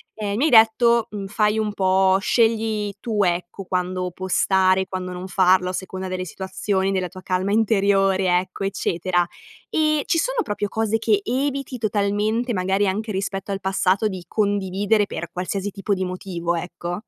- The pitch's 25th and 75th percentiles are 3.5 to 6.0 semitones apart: No, narrow, 2.5 semitones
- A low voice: No, high, 195 Hz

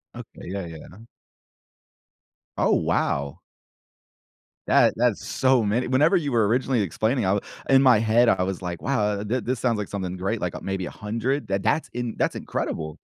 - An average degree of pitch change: Yes, average, 4.7 semitones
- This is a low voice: Yes, low, 110 Hz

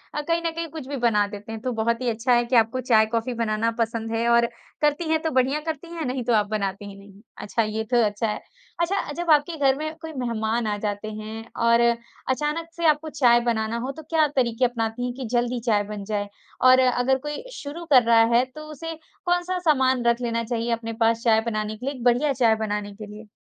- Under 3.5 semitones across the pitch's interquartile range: No, average, 4.3 semitones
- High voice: Yes, high, 240 Hz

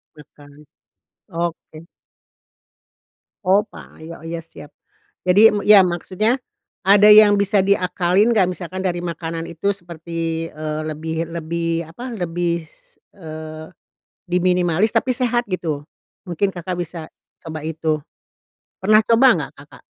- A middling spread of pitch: Yes, average, 3.5 semitones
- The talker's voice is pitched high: No, medium, 175 Hz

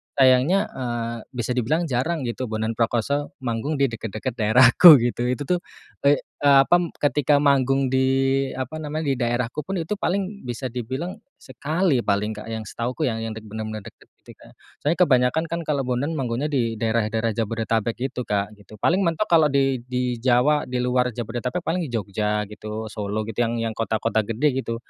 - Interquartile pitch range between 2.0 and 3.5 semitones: No, average, 4.1 semitones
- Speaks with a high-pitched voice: No, low, 125 Hz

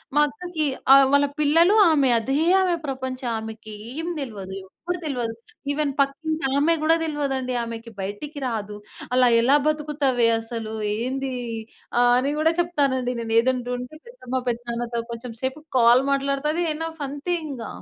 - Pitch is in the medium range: No, very high, 270 Hz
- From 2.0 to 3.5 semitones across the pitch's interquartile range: No, average, 3.9 semitones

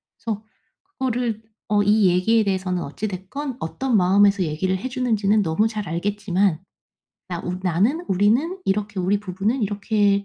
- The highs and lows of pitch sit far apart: No, average, 3.0 semitones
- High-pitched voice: Yes, high, 205 Hz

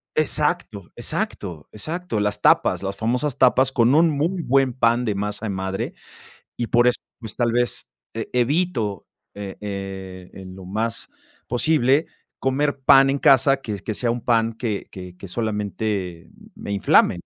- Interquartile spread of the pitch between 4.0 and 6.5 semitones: Yes, average, 5.0 semitones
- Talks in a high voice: No, low, 115 Hz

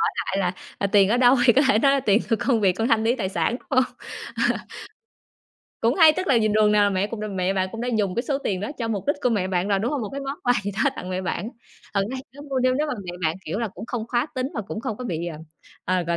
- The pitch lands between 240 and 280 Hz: No, high, 220 Hz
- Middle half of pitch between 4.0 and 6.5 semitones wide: Yes, average, 4.6 semitones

